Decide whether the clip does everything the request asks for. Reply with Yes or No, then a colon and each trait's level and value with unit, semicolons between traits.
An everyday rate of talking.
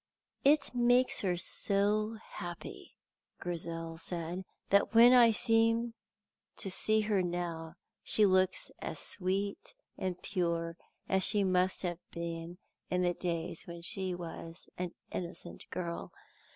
No: slow, 125 wpm